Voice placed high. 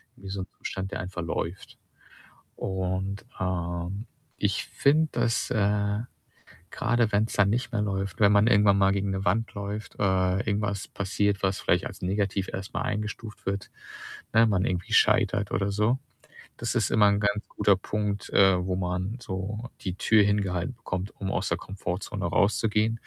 No: low, 100 Hz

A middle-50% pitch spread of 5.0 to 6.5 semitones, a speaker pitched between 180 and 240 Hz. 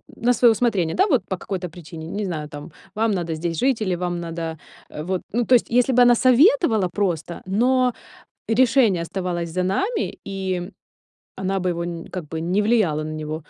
Yes: wide, 5.6 semitones; medium, 185 Hz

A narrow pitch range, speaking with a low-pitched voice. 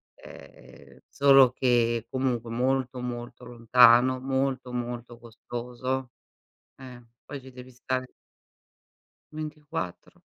Yes: narrow, 1.7 semitones; low, 125 Hz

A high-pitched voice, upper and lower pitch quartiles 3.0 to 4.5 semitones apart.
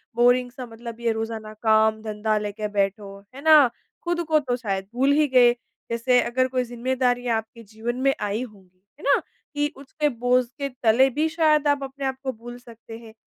Yes: high, 245 Hz; average, 3.3 semitones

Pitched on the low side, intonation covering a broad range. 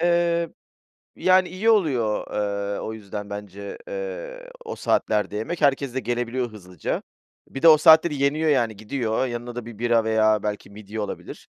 Yes: low, 120 Hz; wide, 7.5 semitones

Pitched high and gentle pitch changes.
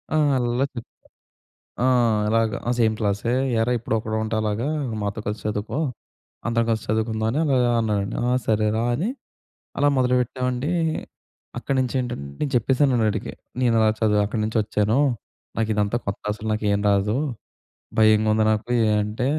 No: low, 110 Hz; narrow, 2.3 semitones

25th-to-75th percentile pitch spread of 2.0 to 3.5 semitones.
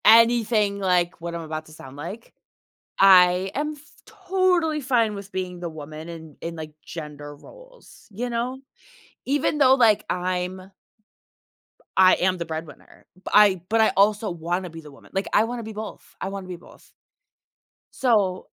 No: average, 5.3 semitones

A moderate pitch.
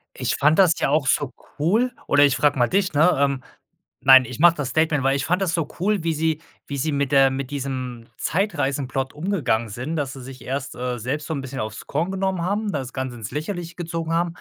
Yes: medium, 145 Hz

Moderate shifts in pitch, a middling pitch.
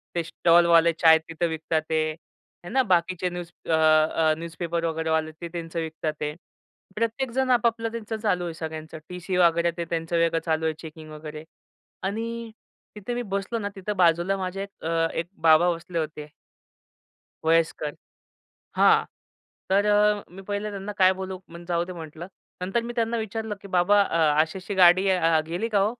Yes: average, 3.8 semitones; medium, 170 Hz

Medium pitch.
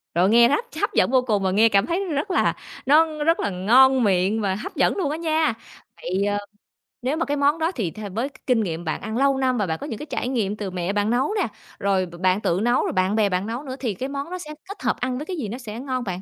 No: high, 235 Hz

